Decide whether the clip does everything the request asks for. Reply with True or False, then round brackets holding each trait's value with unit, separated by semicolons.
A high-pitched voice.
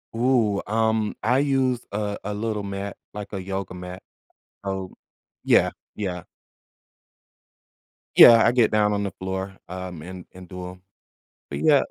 False (100 Hz)